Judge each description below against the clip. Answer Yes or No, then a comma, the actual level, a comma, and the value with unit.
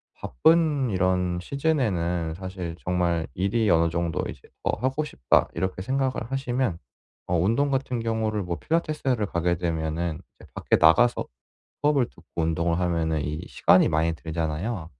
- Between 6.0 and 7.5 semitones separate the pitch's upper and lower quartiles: Yes, wide, 6.8 semitones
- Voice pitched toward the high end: No, very low, 90 Hz